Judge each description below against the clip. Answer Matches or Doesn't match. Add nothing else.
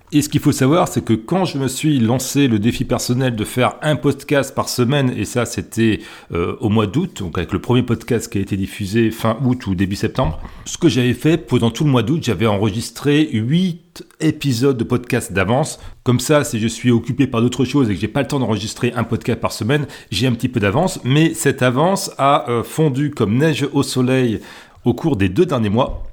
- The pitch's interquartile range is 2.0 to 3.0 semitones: Doesn't match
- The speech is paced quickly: Matches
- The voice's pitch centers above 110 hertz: Matches